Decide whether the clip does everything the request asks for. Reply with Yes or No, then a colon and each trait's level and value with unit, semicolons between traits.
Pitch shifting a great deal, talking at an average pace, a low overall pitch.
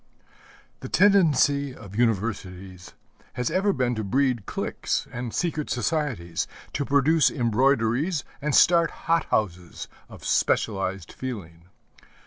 No: wide, 6.7 semitones; slow, 110 wpm; low, 125 Hz